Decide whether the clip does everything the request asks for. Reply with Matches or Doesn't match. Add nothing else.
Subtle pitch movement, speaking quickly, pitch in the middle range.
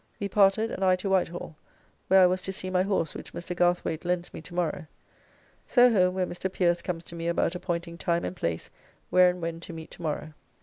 Matches